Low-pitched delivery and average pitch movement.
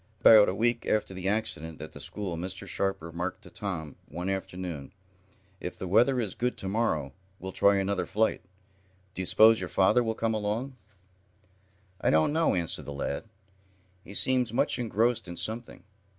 Yes: low, 100 Hz; average, 4.0 semitones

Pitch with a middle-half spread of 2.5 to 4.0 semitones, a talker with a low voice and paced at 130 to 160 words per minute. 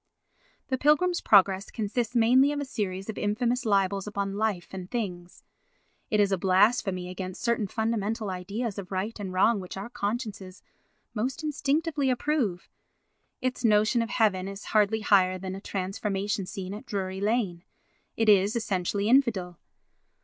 No: average, 3.6 semitones; high, 205 Hz; average, 150 wpm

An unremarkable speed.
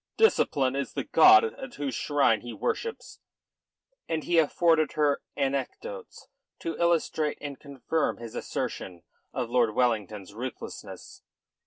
No: slow, 125 wpm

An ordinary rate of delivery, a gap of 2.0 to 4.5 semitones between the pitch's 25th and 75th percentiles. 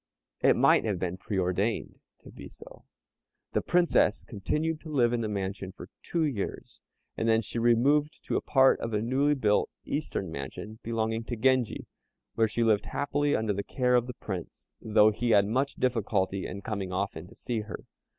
Yes: average, 190 wpm; average, 4.1 semitones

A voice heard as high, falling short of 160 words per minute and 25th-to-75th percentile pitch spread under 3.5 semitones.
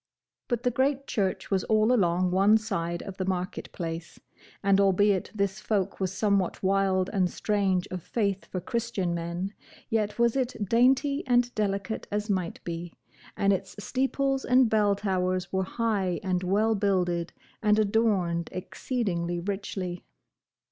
Yes: high, 195 Hz; average, 150 wpm; average, 3.1 semitones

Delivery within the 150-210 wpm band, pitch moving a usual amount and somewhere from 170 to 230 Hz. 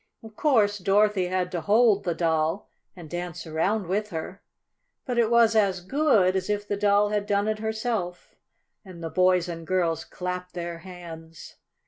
Yes: average, 170 wpm; average, 3.2 semitones; medium, 185 Hz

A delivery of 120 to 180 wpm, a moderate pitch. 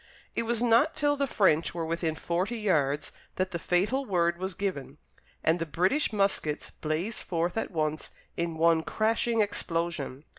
Yes: average, 160 wpm; medium, 175 Hz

